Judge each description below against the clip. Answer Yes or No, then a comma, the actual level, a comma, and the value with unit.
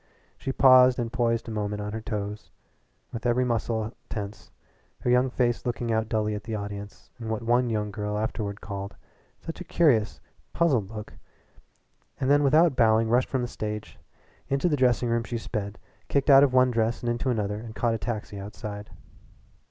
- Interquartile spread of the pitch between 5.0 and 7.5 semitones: No, average, 3.0 semitones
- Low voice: Yes, low, 115 Hz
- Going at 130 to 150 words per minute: No, average, 185 wpm